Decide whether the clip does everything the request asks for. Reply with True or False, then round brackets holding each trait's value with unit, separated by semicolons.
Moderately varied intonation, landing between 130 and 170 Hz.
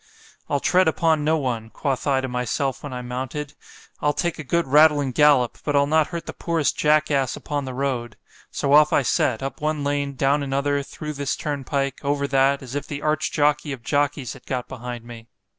False (2.1 semitones; 140 Hz)